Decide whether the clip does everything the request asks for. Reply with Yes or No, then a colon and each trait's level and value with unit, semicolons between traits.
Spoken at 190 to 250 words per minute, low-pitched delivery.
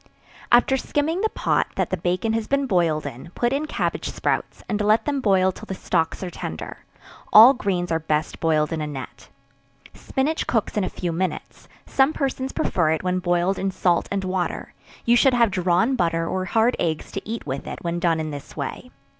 No: fast, 205 wpm; medium, 185 Hz